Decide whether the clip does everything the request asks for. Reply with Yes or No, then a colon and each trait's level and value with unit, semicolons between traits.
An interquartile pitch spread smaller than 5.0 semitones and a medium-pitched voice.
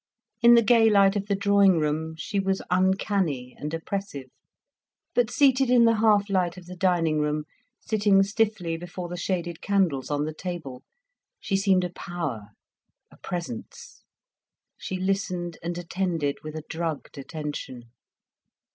Yes: average, 4.0 semitones; medium, 180 Hz